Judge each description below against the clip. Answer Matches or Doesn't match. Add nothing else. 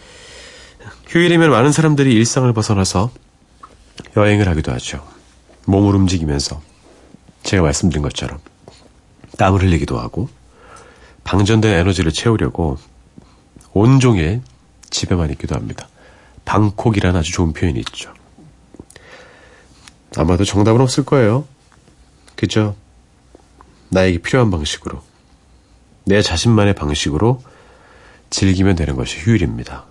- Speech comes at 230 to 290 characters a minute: Matches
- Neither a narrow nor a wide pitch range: Doesn't match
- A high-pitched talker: Doesn't match